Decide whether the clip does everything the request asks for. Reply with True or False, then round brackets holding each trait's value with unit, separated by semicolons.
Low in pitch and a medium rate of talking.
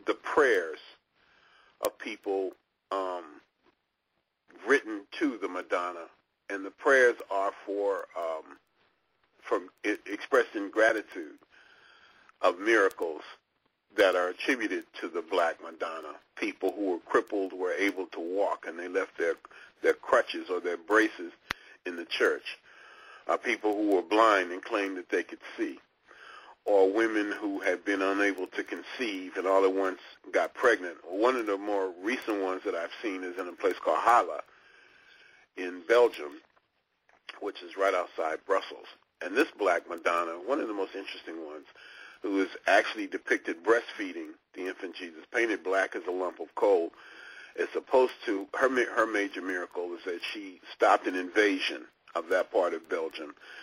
False (360 Hz; 155 wpm)